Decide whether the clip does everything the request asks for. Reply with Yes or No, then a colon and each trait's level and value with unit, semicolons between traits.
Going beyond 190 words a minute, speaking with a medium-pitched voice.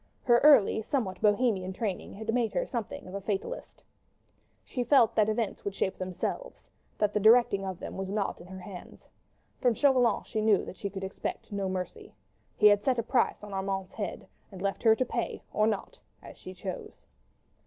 No: average, 200 wpm; high, 210 Hz